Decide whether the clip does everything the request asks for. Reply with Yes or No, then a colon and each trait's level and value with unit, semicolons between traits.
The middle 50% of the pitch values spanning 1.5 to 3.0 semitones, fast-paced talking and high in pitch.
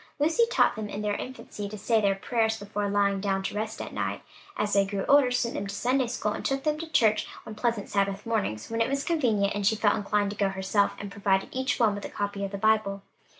Yes: average, 2.7 semitones; fast, 245 wpm; high, 210 Hz